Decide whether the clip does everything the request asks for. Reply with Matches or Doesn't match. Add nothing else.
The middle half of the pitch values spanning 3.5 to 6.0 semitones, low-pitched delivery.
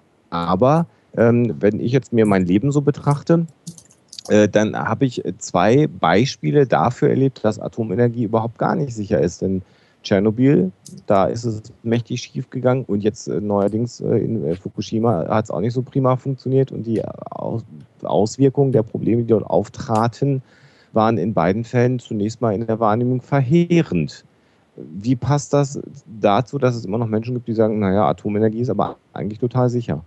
Matches